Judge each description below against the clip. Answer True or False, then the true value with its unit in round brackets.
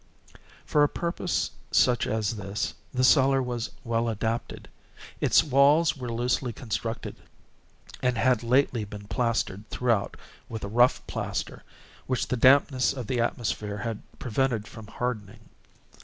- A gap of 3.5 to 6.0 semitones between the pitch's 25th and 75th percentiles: False (2.7 semitones)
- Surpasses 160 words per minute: False (135 wpm)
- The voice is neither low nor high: False (120 Hz)